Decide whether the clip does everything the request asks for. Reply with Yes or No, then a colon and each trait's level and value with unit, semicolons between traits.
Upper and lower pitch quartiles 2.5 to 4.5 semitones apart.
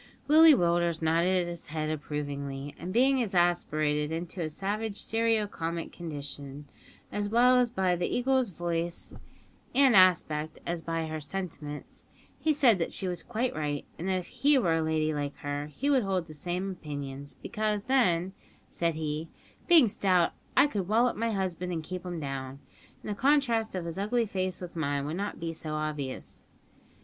No: average, 5.2 semitones